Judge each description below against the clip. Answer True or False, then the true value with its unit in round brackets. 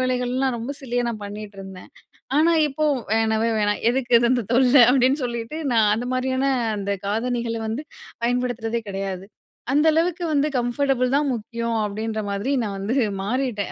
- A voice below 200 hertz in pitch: False (240 Hz)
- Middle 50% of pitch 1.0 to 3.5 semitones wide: True (3.1 semitones)